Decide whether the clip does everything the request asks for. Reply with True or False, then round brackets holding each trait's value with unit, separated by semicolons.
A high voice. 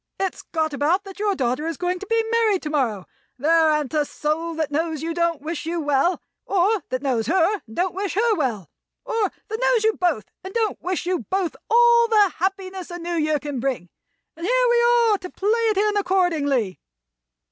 True (350 Hz)